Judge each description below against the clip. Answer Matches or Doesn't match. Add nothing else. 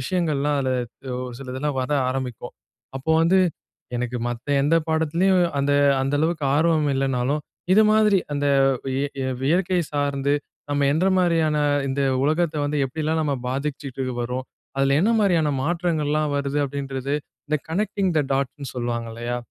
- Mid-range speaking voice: Matches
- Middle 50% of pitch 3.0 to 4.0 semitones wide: Matches